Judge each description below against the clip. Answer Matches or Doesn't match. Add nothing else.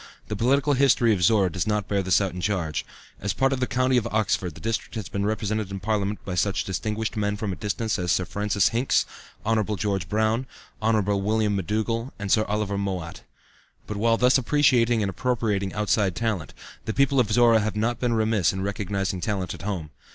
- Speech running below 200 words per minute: Doesn't match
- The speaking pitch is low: Matches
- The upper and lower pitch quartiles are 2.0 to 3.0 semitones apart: Matches